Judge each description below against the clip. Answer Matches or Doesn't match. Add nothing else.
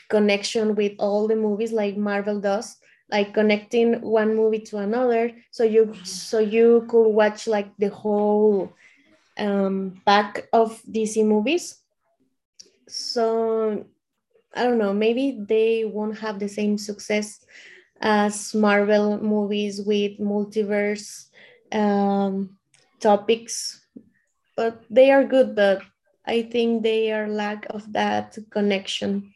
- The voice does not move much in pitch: Matches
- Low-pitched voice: Doesn't match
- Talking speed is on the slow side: Matches